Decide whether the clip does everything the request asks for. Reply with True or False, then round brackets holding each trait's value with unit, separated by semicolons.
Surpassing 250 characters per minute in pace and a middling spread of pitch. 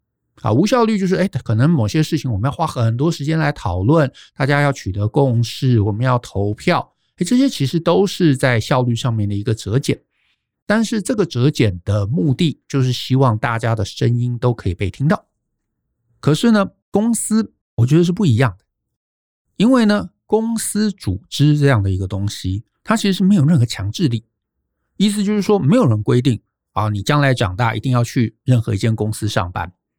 False (290 characters per minute; 7.0 semitones)